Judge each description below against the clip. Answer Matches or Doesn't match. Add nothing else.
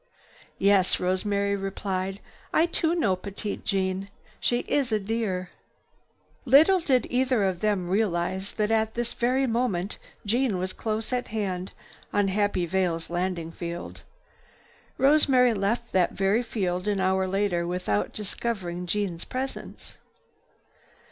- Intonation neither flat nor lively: Matches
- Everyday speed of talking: Doesn't match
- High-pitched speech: Matches